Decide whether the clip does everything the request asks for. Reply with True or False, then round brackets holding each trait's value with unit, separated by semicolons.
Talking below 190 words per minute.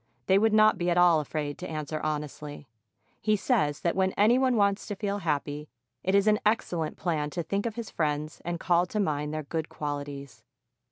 False (205 wpm)